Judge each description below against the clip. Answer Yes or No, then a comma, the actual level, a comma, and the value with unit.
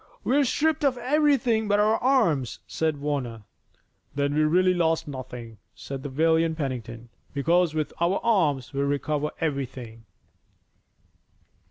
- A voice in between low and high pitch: Yes, medium, 155 Hz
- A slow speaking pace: Yes, slow, 130 wpm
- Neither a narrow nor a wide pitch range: No, wide, 7.1 semitones